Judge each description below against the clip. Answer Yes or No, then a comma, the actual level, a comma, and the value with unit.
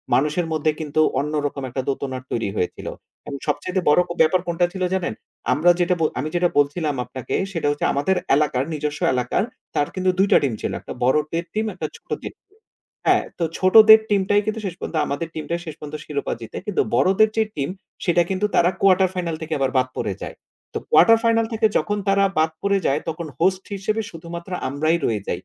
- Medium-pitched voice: Yes, medium, 165 Hz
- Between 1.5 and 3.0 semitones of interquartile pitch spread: No, average, 4.7 semitones